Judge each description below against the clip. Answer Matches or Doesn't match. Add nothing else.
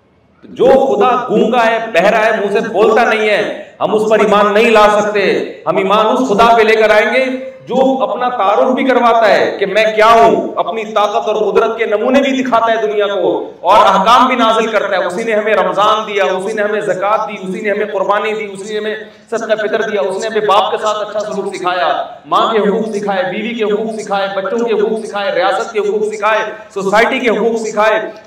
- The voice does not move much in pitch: Matches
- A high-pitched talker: Matches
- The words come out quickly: Matches